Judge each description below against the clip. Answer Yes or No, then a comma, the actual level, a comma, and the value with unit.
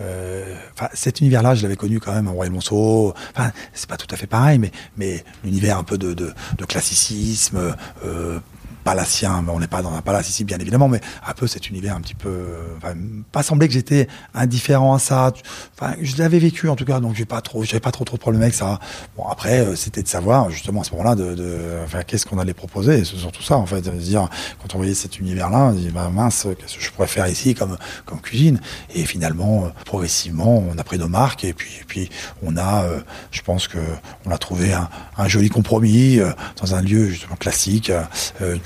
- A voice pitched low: Yes, low, 100 Hz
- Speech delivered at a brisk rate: Yes, fast, 225 wpm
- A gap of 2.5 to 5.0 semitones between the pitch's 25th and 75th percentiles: Yes, average, 4.6 semitones